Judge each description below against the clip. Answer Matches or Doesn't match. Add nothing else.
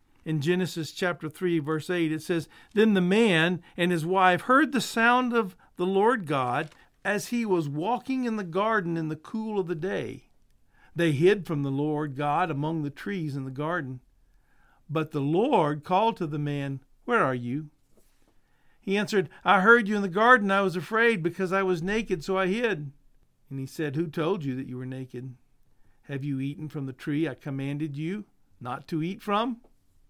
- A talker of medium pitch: Matches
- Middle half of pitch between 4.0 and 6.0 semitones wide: Matches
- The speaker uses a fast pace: Doesn't match